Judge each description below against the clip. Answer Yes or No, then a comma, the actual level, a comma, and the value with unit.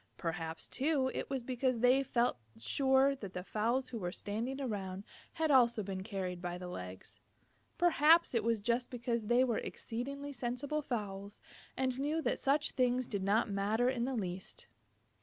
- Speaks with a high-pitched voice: Yes, high, 240 Hz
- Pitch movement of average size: Yes, average, 4.9 semitones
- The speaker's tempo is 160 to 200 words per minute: Yes, average, 170 wpm